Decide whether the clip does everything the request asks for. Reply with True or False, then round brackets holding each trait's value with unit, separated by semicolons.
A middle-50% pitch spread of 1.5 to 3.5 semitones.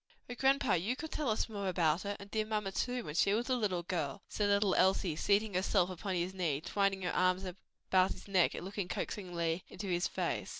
True (2.8 semitones)